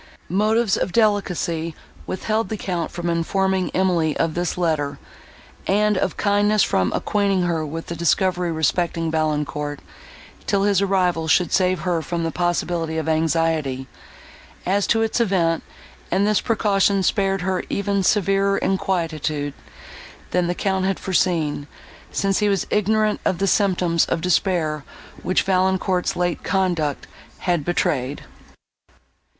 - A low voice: No, medium, 180 Hz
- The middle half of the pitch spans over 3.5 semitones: No, average, 3.2 semitones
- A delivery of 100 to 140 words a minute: Yes, slow, 135 wpm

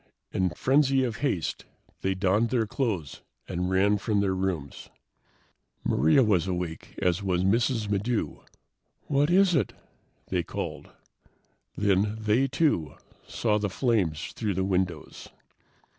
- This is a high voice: No, low, 100 Hz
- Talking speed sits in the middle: No, slow, 130 wpm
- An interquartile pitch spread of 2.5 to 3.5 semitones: No, average, 4.3 semitones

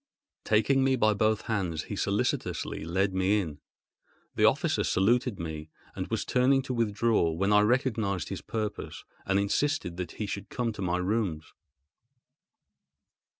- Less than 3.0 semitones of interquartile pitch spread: No, average, 4.1 semitones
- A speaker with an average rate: Yes, average, 150 wpm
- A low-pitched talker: Yes, low, 105 Hz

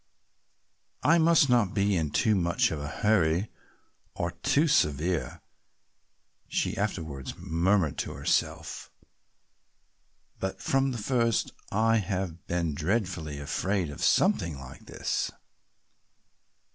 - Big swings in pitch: Yes, wide, 5.7 semitones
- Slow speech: Yes, slow, 110 wpm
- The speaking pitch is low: Yes, very low, 95 Hz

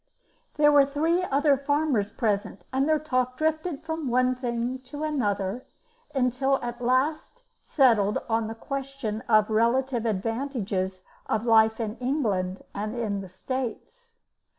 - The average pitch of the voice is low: No, very high, 250 Hz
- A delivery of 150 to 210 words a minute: No, average, 140 wpm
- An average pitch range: Yes, average, 4.3 semitones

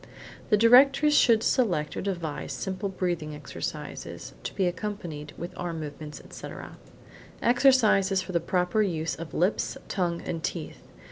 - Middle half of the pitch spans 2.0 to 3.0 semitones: No, average, 4.4 semitones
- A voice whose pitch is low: No, medium, 180 Hz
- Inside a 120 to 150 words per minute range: Yes, slow, 135 wpm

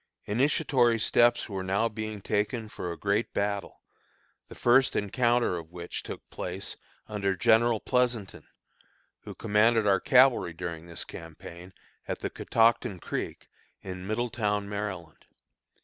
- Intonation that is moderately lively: Yes, average, 3.9 semitones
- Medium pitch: No, low, 105 Hz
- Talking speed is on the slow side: Yes, slow, 130 wpm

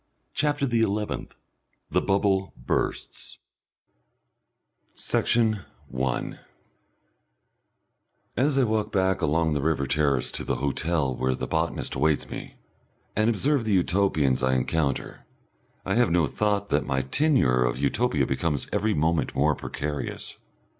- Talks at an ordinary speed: No, slow, 125 wpm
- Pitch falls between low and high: No, very low, 85 Hz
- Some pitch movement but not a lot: No, wide, 7.5 semitones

